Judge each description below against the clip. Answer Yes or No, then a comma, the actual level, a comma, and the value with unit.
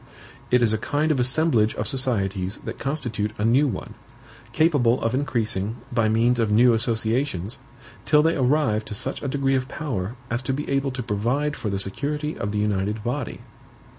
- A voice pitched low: Yes, low, 120 Hz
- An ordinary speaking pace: Yes, average, 185 wpm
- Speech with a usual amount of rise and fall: Yes, average, 4.4 semitones